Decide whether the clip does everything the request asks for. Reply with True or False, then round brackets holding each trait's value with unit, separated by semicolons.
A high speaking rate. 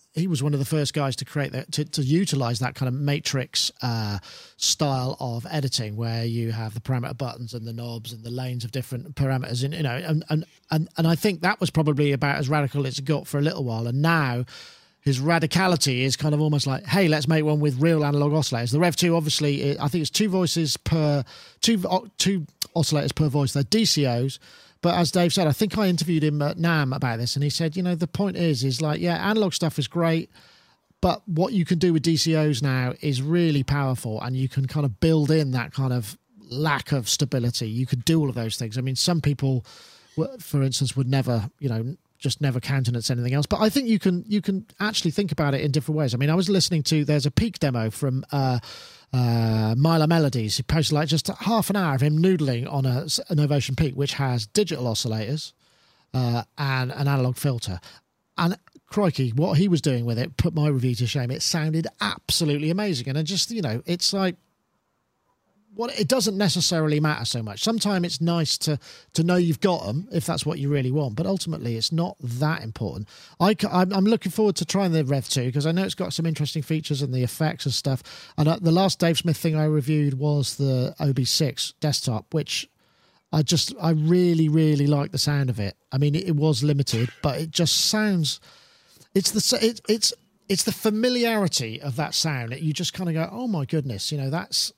True (220 wpm)